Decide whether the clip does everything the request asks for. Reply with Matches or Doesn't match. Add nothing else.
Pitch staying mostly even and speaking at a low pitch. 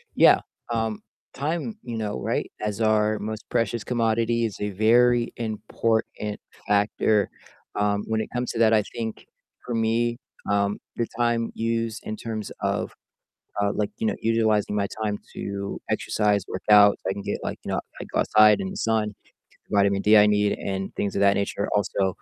Matches